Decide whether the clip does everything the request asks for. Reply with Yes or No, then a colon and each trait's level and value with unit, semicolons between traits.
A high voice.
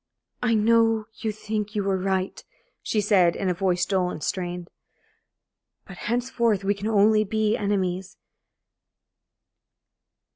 Yes: high, 205 Hz